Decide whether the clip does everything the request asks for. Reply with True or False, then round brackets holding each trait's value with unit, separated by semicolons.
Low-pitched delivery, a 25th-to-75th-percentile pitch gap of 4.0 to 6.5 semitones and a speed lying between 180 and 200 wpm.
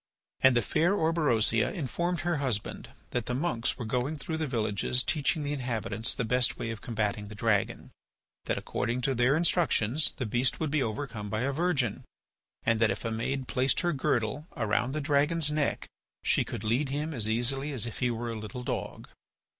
True (125 Hz; 4.6 semitones; 195 wpm)